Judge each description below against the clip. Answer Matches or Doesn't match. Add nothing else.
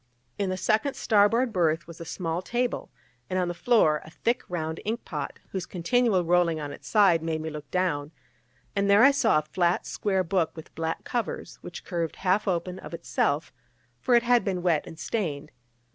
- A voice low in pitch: Doesn't match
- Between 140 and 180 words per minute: Doesn't match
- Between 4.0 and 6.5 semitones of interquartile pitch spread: Matches